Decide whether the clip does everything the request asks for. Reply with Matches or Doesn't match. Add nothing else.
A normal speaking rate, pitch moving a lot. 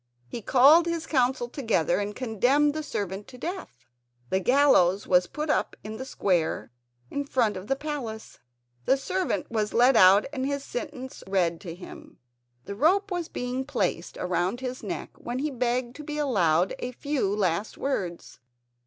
Matches